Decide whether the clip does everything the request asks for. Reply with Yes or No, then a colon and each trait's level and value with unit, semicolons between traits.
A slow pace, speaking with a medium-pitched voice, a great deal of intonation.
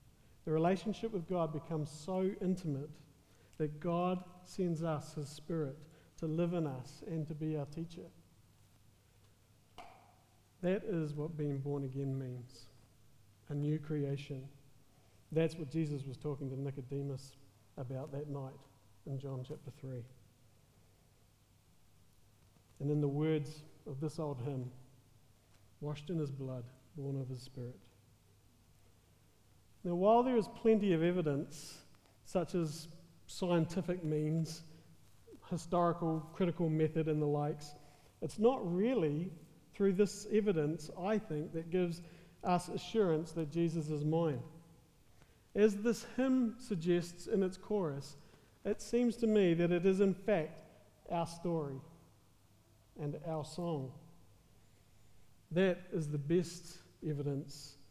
No: slow, 125 wpm; medium, 150 Hz; average, 5.0 semitones